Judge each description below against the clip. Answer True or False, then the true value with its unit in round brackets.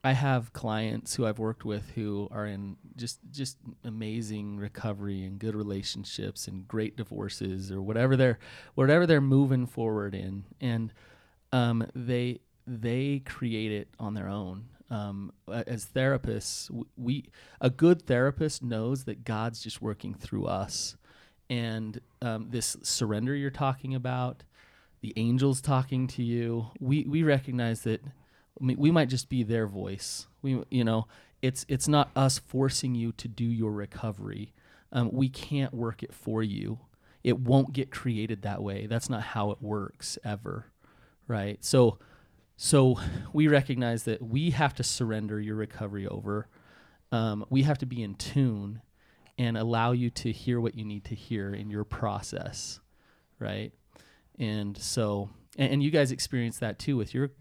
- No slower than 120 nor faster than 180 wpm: True (160 wpm)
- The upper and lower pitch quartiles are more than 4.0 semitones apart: False (3.5 semitones)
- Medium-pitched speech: False (115 Hz)